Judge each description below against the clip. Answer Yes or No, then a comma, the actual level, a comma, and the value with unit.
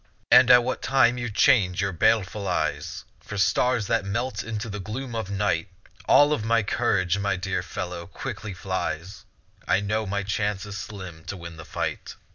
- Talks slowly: No, average, 180 wpm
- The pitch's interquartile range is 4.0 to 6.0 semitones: No, average, 3.6 semitones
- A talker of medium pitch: No, low, 100 Hz